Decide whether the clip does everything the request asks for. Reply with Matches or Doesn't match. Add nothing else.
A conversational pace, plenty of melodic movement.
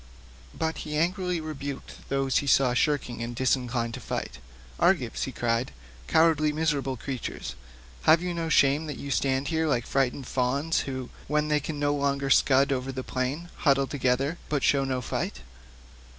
Doesn't match